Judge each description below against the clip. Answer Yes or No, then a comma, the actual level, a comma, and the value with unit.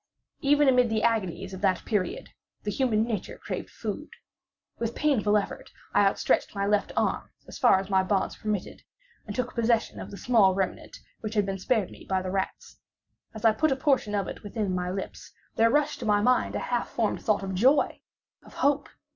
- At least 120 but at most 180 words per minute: No, average, 195 wpm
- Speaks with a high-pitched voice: Yes, high, 210 Hz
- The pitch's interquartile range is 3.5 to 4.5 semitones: Yes, average, 3.8 semitones